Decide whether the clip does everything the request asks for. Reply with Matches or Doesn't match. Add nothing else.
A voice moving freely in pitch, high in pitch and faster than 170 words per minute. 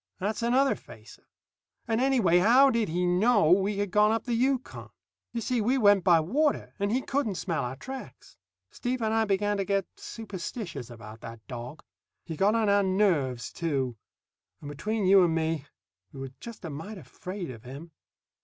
Matches